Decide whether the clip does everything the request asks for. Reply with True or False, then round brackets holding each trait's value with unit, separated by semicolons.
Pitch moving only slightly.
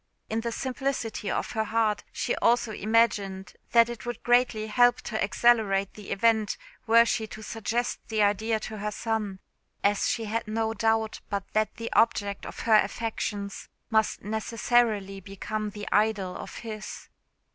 True (1.8 semitones)